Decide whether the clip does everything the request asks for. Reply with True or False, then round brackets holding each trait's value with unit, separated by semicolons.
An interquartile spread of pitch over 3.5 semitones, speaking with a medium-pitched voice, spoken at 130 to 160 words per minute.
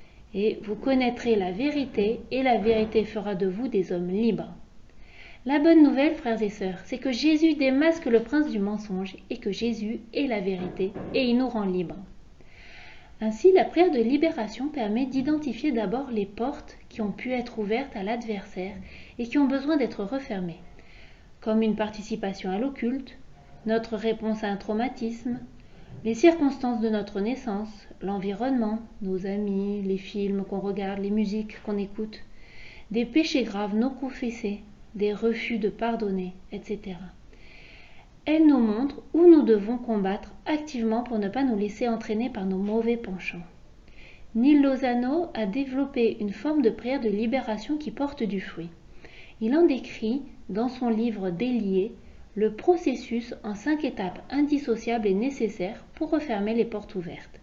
False (4.0 semitones; 225 Hz; 155 wpm)